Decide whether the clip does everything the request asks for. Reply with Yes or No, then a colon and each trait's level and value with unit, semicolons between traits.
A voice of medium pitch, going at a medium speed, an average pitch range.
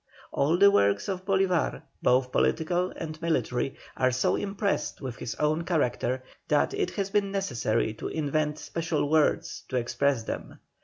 No: medium, 155 Hz; average, 155 wpm; wide, 6.3 semitones